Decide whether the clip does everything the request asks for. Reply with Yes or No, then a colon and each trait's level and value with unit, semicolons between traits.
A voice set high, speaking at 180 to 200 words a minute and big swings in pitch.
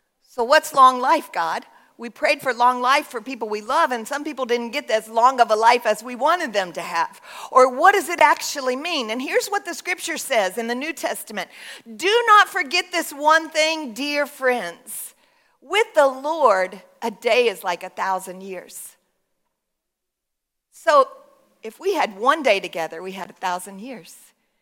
Yes: very high, 260 Hz; average, 185 wpm; wide, 6.0 semitones